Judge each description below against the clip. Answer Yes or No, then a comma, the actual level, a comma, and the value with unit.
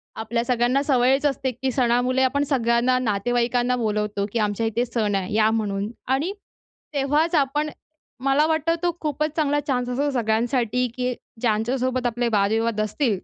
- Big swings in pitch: No, average, 3.4 semitones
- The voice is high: Yes, high, 245 Hz